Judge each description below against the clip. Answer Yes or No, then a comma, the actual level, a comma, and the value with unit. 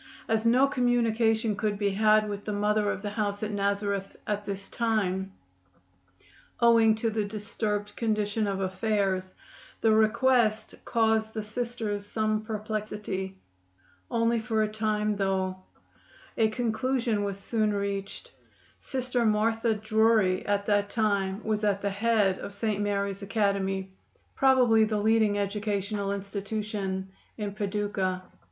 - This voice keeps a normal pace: No, slow, 130 wpm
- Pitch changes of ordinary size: No, narrow, 1.7 semitones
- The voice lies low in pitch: No, high, 210 Hz